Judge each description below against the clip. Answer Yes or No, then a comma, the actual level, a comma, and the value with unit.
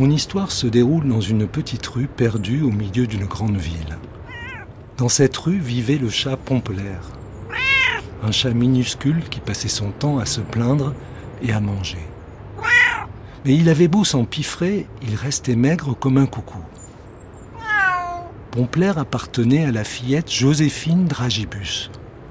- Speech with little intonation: No, average, 4.9 semitones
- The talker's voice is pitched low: Yes, low, 125 Hz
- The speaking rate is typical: No, slow, 140 wpm